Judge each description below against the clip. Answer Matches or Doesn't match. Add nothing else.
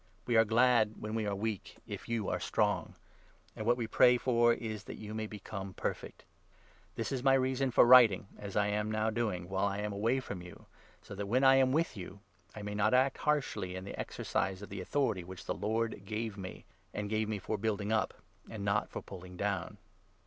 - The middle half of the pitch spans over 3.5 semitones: Doesn't match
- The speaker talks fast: Matches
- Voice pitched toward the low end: Matches